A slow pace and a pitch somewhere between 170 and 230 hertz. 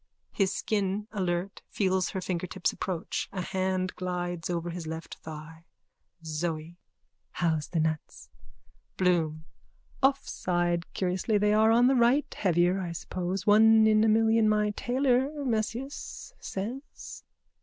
Yes: slow, 130 wpm; medium, 185 Hz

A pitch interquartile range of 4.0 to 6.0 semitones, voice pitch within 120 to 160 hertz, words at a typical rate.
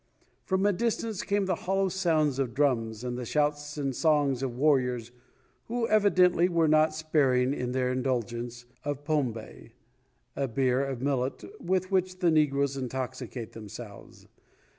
Yes: average, 5.1 semitones; medium, 140 Hz; average, 150 wpm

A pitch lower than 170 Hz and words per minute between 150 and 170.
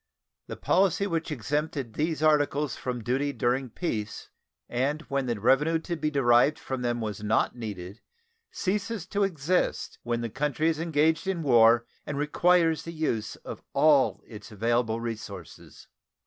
Yes: medium, 140 Hz; average, 155 wpm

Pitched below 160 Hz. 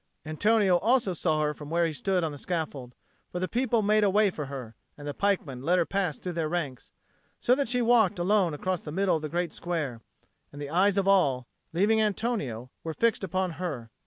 No: medium, 175 Hz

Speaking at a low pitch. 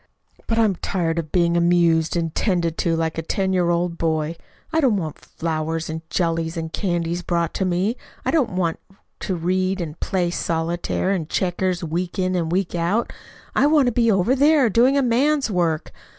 No: medium, 175 Hz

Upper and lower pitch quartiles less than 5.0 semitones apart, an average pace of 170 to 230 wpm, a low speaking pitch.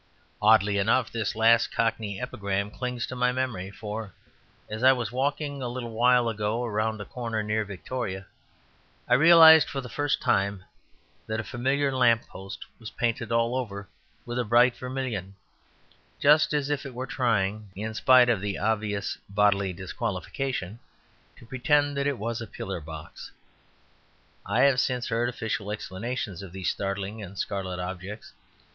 No: average, 3.9 semitones; average, 160 wpm; low, 115 Hz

